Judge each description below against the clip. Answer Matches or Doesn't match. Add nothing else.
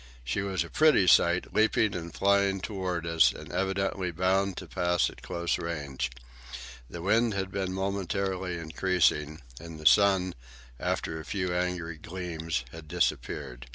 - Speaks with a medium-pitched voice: Doesn't match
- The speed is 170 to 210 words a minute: Doesn't match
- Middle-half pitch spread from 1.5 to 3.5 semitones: Matches